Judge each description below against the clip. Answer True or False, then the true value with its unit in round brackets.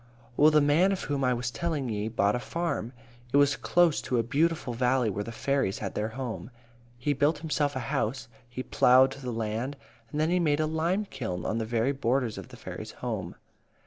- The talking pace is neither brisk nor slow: False (210 wpm)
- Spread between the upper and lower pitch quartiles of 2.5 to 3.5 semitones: False (4.4 semitones)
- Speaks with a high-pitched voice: False (130 Hz)